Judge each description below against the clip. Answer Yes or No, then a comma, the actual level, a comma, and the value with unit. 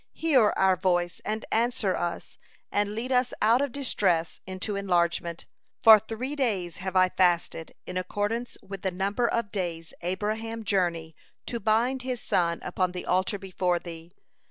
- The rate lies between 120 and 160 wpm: Yes, average, 155 wpm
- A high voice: Yes, high, 195 Hz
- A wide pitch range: No, average, 4.1 semitones